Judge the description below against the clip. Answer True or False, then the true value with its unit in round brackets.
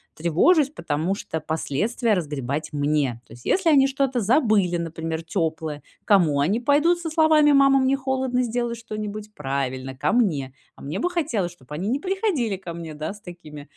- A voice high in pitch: True (195 Hz)